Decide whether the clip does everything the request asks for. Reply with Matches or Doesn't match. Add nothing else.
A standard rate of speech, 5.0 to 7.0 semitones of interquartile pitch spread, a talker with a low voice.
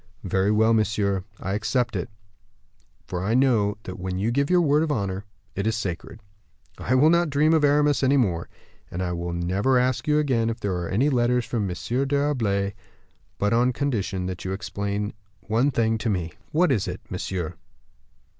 Matches